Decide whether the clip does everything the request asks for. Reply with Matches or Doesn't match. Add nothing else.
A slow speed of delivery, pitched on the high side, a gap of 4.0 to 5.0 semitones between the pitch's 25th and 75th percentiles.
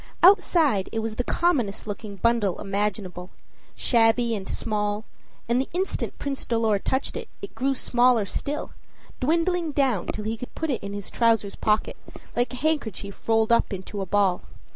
Doesn't match